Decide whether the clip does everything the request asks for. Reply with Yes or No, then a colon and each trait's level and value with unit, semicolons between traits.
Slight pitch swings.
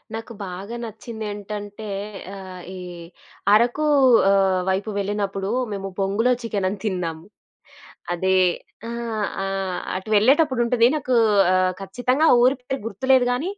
No: average, 3.6 semitones